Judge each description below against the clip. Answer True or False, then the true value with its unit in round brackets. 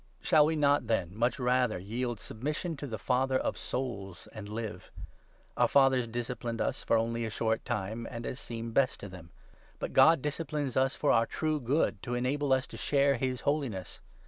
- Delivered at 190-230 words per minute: True (195 wpm)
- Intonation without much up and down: False (3.5 semitones)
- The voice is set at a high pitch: False (125 Hz)